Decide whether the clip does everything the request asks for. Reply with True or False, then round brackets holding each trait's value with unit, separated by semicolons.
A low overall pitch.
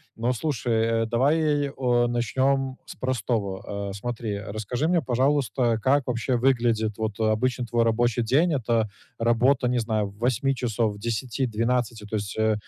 True (120 Hz)